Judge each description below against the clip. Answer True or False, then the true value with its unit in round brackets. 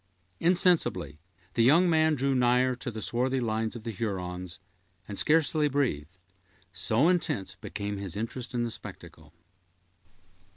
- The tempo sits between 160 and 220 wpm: False (135 wpm)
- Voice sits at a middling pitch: False (120 Hz)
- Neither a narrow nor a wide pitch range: False (6.1 semitones)